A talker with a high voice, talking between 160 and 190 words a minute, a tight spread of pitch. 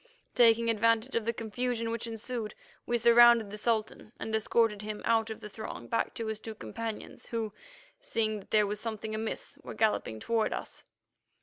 Yes: high, 225 Hz; average, 180 wpm; narrow, 1.3 semitones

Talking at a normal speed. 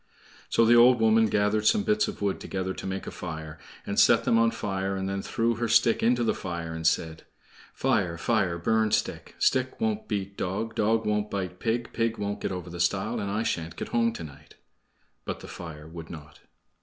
No: fast, 210 wpm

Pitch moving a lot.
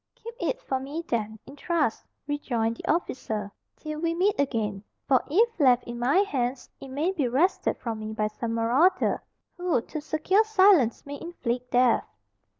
Yes: wide, 6.3 semitones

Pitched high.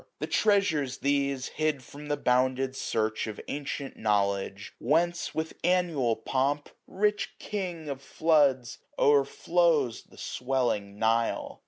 No: medium, 140 Hz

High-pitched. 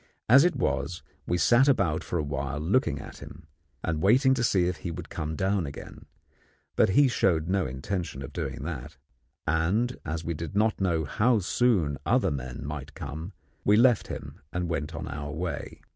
No: very low, 85 Hz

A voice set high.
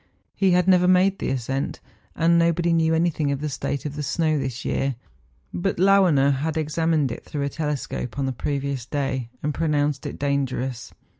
No: medium, 145 Hz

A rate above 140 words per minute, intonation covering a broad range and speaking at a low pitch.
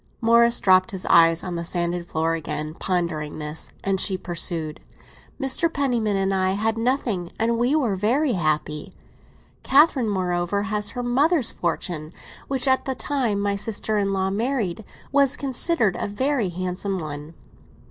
No: average, 155 wpm; wide, 5.7 semitones; high, 200 Hz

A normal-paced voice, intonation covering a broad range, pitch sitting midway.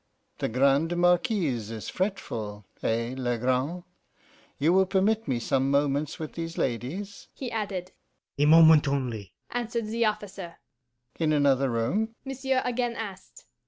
No: slow, 130 wpm; wide, 7.8 semitones; medium, 165 Hz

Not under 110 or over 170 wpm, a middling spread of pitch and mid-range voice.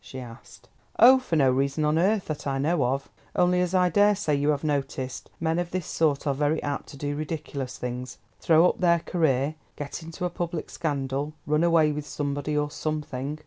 No: average, 200 wpm; average, 3.2 semitones; medium, 150 Hz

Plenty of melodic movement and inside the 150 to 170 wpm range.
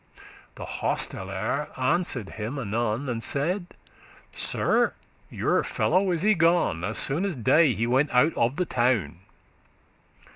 No: wide, 6.5 semitones; slow, 135 wpm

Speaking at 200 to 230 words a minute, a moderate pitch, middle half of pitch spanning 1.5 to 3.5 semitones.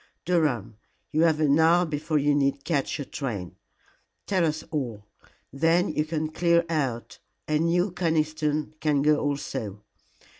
No: average, 145 wpm; medium, 155 Hz; average, 2.8 semitones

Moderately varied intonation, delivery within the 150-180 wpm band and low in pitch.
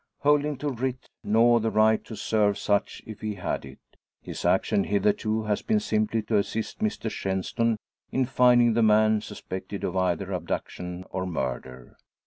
Yes: average, 3.1 semitones; average, 160 wpm; low, 110 Hz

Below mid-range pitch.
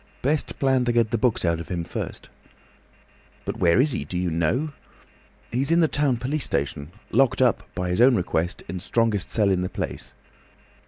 Yes: low, 115 Hz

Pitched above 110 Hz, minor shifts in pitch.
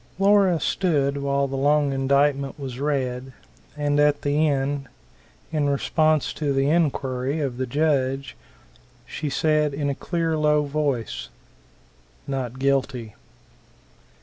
Yes: medium, 140 Hz; narrow, 2.0 semitones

